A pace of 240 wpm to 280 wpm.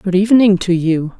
No: average, 200 wpm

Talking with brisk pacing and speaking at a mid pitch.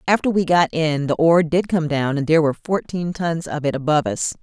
Yes: fast, 245 wpm; medium, 160 Hz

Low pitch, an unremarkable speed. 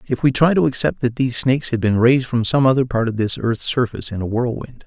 No: low, 125 Hz; fast, 270 wpm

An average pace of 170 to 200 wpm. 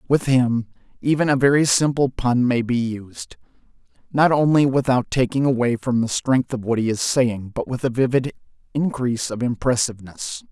Yes: average, 175 wpm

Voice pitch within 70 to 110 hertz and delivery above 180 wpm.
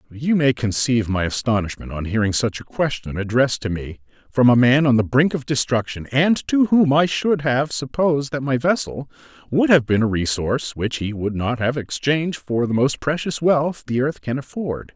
No: low, 130 Hz; fast, 205 wpm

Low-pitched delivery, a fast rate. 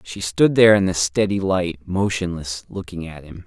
No: very low, 90 Hz; average, 190 wpm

